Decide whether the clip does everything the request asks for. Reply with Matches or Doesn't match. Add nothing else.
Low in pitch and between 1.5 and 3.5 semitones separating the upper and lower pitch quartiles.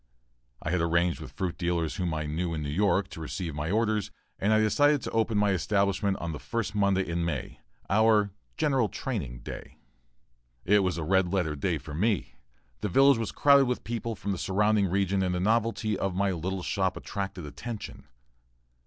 Doesn't match